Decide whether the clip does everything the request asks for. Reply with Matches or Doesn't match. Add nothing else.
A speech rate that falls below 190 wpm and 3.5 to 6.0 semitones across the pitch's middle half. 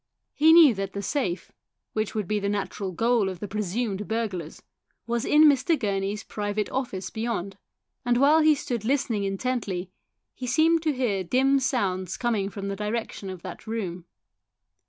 Matches